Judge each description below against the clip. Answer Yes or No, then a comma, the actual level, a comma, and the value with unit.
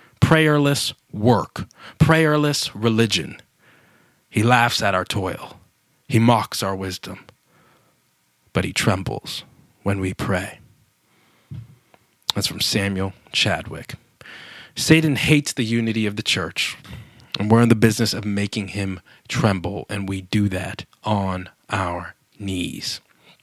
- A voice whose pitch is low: Yes, low, 105 Hz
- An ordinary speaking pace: No, slow, 120 wpm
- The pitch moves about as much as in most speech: Yes, average, 4.1 semitones